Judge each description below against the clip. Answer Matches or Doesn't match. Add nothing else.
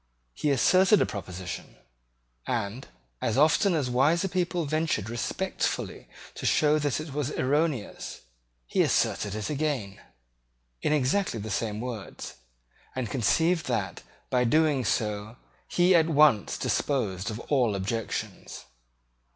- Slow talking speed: Matches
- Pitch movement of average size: Doesn't match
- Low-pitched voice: Matches